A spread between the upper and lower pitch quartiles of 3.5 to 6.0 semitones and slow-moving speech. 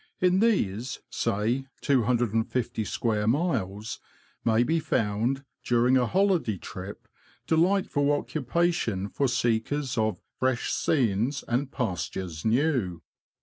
Yes: average, 4.8 semitones; slow, 105 wpm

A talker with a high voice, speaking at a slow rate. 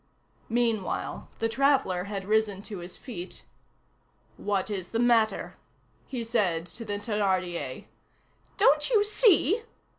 Yes: high, 215 Hz; slow, 120 wpm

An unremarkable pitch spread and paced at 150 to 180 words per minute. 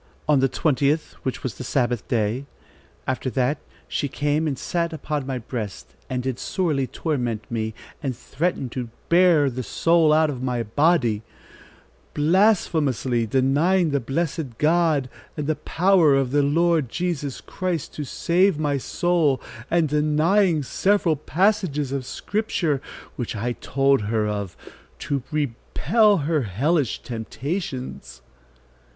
No: average, 4.6 semitones; slow, 135 wpm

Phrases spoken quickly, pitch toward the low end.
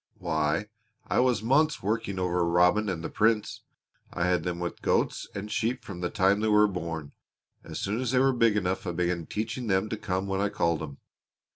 Yes: fast, 210 wpm; very low, 95 Hz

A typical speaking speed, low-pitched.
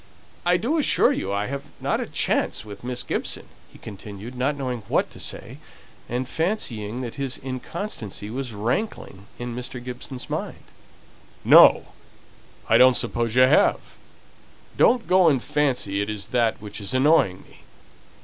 Yes: average, 150 wpm; low, 125 Hz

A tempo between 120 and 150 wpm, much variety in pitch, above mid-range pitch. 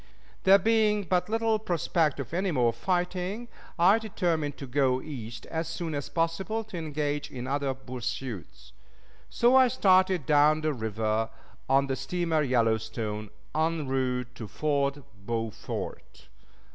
No: slow, 135 wpm; wide, 6.0 semitones; medium, 150 Hz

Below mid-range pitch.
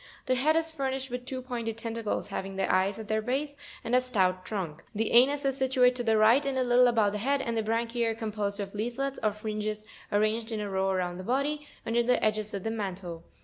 No: high, 225 Hz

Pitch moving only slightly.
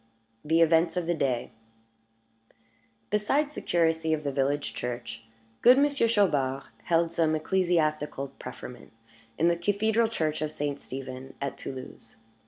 No: average, 4.3 semitones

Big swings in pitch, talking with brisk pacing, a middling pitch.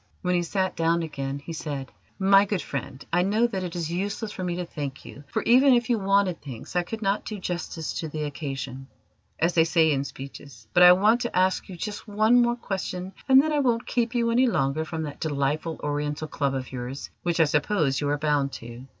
Yes: wide, 5.8 semitones; fast, 225 wpm; medium, 170 Hz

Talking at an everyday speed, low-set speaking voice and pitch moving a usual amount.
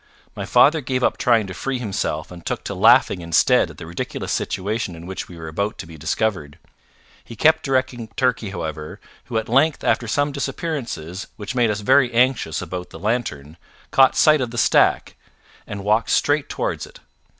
No: average, 185 wpm; low, 110 Hz; wide, 6.6 semitones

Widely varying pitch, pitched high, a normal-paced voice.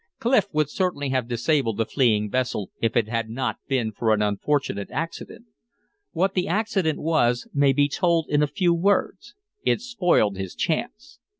No: wide, 7.2 semitones; medium, 145 Hz; average, 170 wpm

